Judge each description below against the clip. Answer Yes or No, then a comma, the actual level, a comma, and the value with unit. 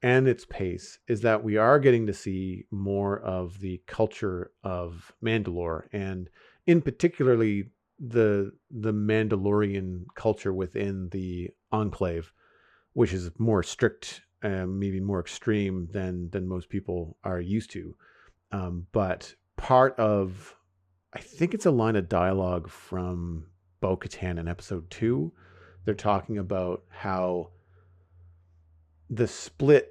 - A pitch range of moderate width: Yes, average, 3.3 semitones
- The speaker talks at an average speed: No, slow, 125 wpm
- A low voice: Yes, very low, 95 Hz